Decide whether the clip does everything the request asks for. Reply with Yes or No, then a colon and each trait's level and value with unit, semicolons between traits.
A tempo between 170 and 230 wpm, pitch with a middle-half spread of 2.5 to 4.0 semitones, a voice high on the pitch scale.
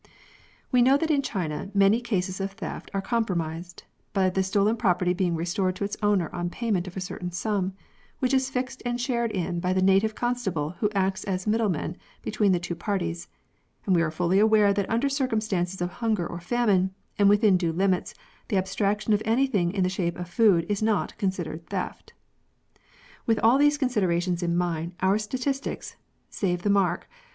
Yes: average, 185 wpm; average, 3.7 semitones; high, 195 Hz